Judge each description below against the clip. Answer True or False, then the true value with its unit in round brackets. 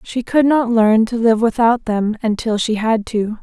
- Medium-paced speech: False (210 wpm)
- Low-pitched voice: False (225 Hz)